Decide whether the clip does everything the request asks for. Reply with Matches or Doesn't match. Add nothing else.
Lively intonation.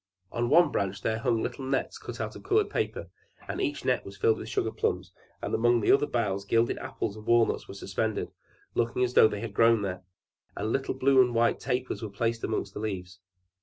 Doesn't match